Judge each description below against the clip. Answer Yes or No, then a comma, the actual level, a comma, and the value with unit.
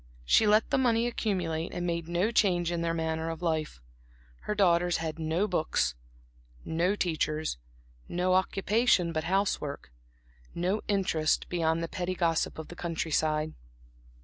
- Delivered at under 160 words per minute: Yes, average, 150 wpm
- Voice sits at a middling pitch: Yes, medium, 170 Hz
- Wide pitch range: No, average, 2.7 semitones